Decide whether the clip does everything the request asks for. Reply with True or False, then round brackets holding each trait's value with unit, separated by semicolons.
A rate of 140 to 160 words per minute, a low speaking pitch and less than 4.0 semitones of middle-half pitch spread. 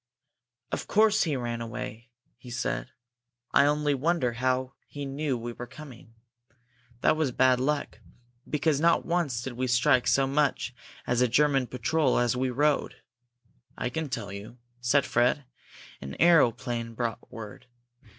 True (150 wpm; 130 Hz; 3.5 semitones)